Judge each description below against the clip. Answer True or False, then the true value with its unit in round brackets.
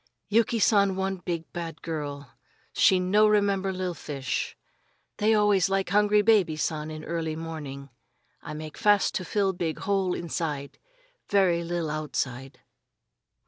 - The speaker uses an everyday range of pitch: True (4.3 semitones)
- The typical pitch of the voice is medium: True (175 Hz)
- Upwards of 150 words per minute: False (140 wpm)